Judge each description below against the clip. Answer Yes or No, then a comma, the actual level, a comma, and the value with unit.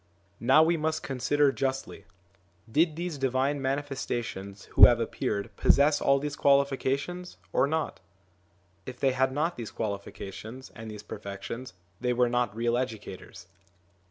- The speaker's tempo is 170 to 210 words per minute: No, average, 145 wpm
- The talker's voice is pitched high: No, low, 130 Hz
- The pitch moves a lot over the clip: No, average, 3.7 semitones